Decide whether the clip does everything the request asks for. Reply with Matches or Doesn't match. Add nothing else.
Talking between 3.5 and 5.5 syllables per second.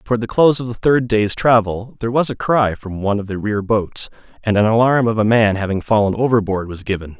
Doesn't match